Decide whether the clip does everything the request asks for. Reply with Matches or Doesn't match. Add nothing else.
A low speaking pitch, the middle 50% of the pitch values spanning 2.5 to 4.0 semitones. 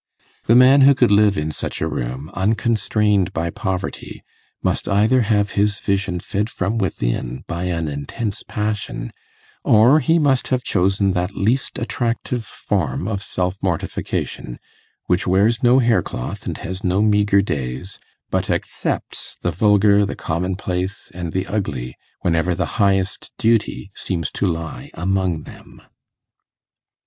Matches